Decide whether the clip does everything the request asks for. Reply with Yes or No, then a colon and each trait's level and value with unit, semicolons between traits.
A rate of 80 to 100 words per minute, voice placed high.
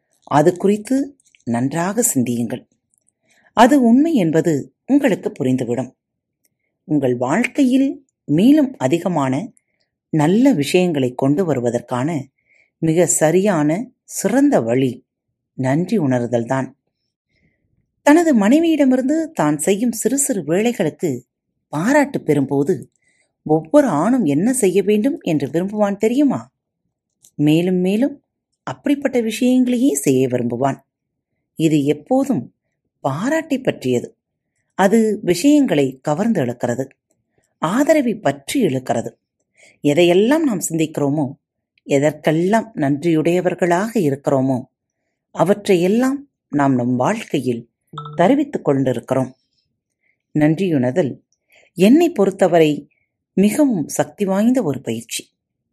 No: average, 85 wpm; medium, 165 Hz